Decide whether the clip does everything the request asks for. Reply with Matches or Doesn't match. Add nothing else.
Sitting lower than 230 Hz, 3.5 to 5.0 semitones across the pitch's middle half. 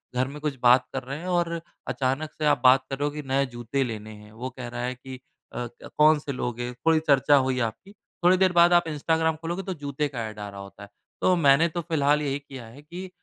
Matches